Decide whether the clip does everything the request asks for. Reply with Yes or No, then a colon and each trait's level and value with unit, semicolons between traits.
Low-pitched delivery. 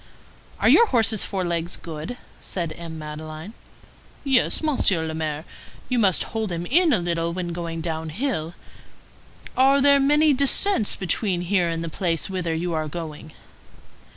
No: medium, 175 Hz